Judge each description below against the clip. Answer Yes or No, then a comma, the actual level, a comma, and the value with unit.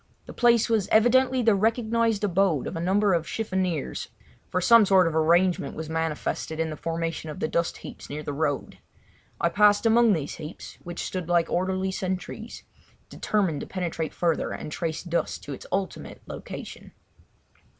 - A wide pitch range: No, average, 4.2 semitones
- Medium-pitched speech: Yes, medium, 180 Hz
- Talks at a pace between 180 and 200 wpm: No, average, 170 wpm